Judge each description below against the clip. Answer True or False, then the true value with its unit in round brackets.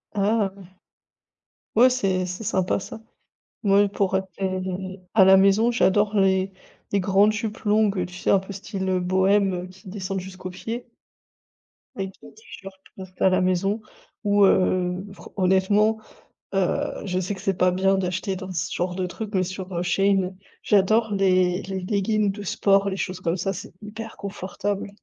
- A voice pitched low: False (190 Hz)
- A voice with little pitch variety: True (1.6 semitones)